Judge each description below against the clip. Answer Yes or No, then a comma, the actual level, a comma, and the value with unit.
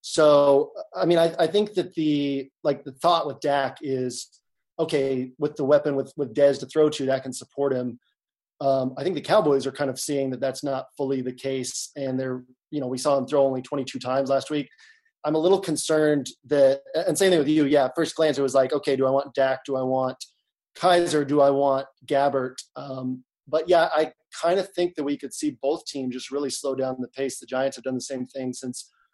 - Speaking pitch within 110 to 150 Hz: Yes, medium, 140 Hz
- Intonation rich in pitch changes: No, narrow, 2.5 semitones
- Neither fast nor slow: No, fast, 235 wpm